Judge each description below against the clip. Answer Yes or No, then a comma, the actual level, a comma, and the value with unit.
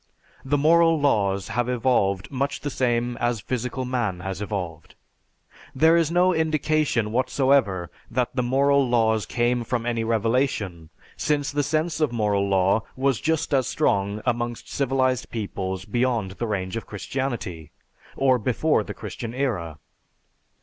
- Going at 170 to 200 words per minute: No, average, 145 wpm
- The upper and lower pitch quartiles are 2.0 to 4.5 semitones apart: No, average, 4.9 semitones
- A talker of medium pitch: No, low, 120 Hz